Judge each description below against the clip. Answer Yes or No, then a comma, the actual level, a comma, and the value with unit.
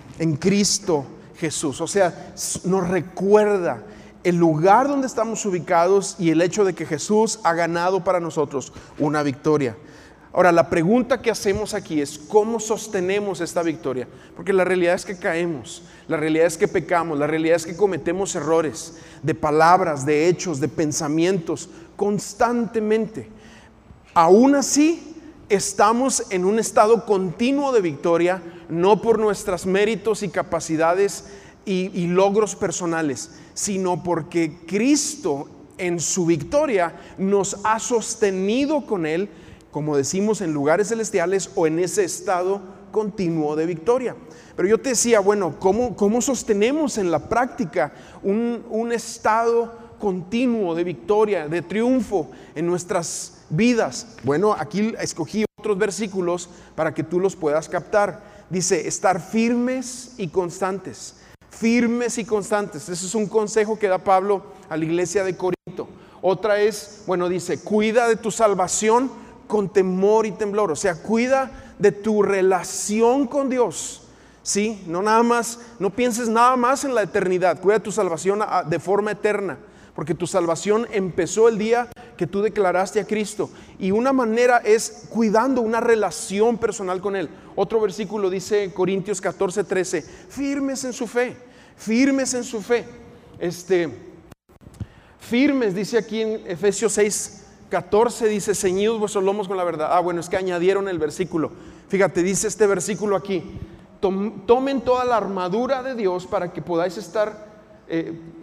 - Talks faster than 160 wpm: No, average, 145 wpm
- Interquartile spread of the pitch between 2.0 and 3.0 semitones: No, average, 4.1 semitones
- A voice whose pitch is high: Yes, high, 195 Hz